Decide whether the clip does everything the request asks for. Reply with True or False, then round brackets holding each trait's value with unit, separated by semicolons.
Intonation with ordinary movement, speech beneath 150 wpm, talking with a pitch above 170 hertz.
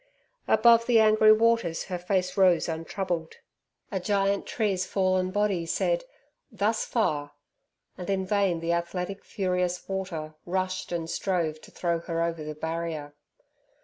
True (3.1 semitones; 140 wpm; 185 Hz)